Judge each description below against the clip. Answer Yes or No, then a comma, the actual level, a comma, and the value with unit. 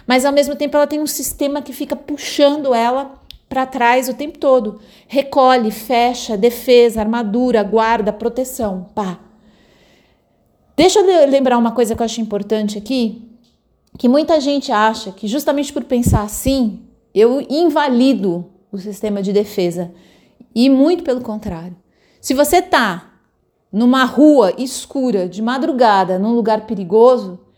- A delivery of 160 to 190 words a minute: No, average, 140 wpm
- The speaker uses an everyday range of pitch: Yes, average, 4.3 semitones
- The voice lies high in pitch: Yes, high, 240 Hz